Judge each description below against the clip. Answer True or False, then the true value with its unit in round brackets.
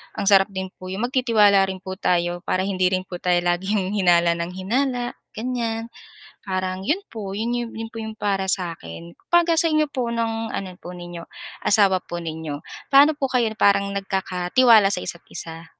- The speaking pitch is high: True (195 Hz)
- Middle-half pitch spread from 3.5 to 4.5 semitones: True (4.1 semitones)